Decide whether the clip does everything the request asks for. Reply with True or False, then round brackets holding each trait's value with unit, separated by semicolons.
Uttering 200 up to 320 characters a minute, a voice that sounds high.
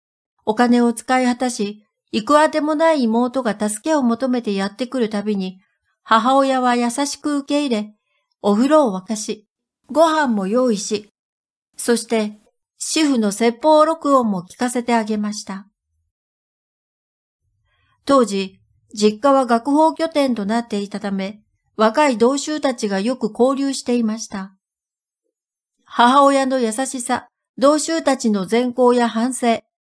True (250 characters per minute; 240 Hz)